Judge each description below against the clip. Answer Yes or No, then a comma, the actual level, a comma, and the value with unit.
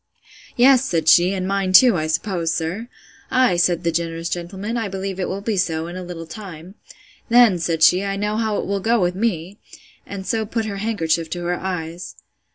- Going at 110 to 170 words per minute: No, average, 200 wpm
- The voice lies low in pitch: No, medium, 185 Hz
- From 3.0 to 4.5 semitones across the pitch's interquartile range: Yes, average, 3.6 semitones